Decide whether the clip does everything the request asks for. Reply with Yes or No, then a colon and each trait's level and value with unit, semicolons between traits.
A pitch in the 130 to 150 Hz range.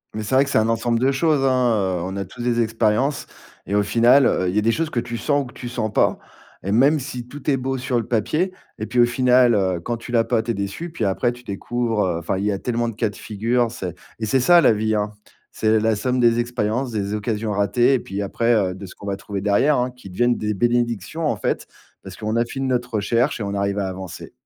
No: low, 115 Hz